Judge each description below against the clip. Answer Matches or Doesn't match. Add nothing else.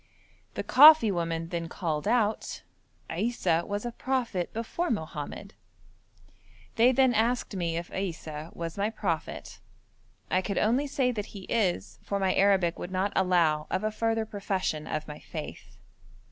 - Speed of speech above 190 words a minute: Doesn't match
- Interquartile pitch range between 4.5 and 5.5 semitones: Matches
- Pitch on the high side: Matches